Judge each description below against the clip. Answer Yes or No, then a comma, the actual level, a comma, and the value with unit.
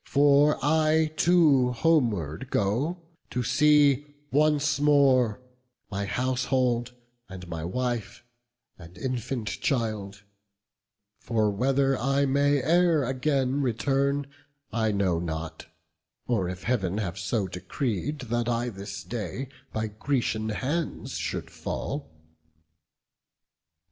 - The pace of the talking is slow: Yes, slow, 105 wpm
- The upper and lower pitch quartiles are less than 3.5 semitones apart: No, wide, 5.5 semitones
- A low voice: Yes, low, 125 Hz